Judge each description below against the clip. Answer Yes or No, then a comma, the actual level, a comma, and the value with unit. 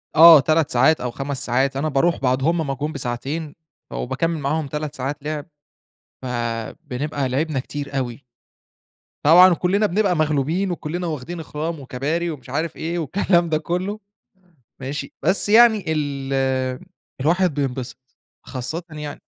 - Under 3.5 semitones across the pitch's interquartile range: No, average, 3.8 semitones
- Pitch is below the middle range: No, medium, 150 Hz